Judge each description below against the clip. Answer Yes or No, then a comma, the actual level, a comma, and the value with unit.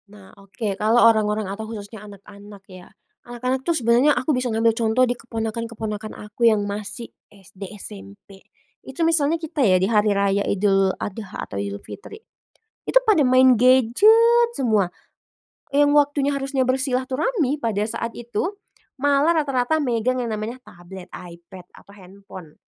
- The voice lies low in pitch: No, high, 230 Hz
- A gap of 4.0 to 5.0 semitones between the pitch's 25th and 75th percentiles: Yes, average, 4.6 semitones